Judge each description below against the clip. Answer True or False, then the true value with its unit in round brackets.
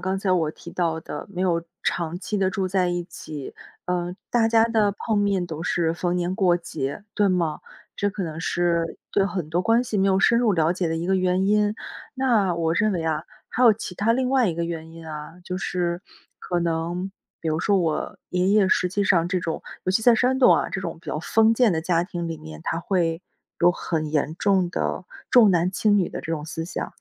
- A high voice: False (180 Hz)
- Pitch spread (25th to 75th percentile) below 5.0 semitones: True (3.4 semitones)